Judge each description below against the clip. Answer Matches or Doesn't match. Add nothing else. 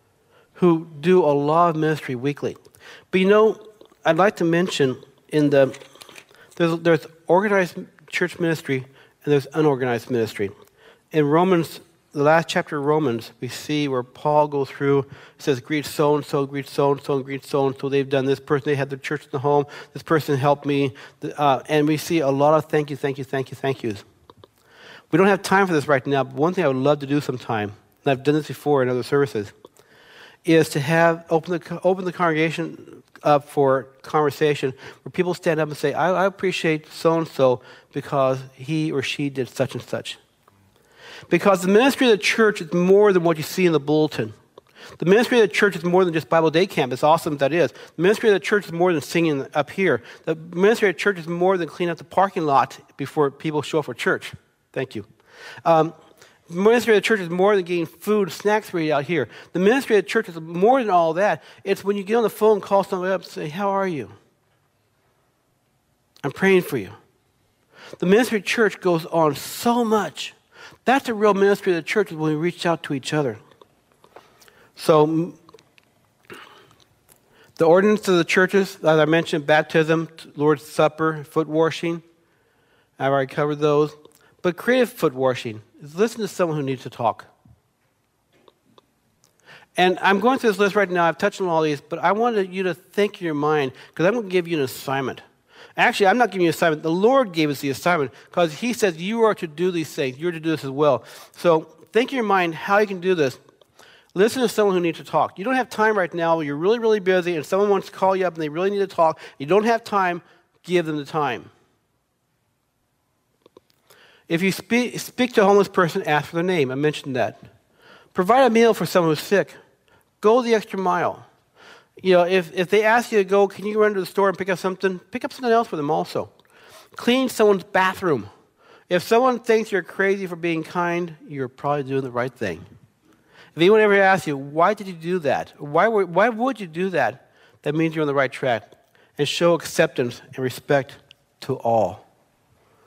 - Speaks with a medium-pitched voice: Matches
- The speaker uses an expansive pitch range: Doesn't match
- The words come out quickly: Matches